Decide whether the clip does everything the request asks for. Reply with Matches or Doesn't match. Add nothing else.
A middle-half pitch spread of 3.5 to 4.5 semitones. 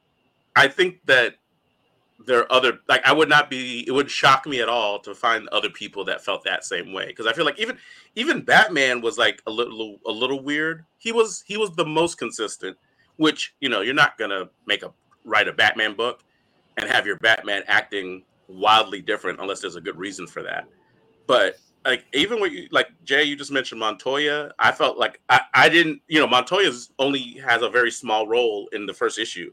Doesn't match